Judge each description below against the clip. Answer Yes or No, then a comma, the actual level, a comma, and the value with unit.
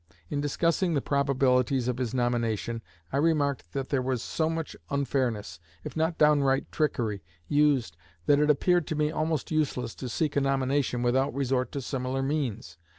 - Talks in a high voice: No, low, 135 Hz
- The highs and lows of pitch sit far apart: No, average, 3.1 semitones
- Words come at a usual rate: Yes, average, 165 wpm